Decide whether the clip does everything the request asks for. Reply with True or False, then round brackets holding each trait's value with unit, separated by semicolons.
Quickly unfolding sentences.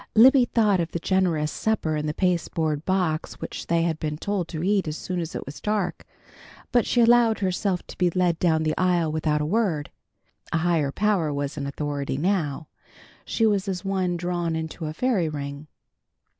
False (190 wpm)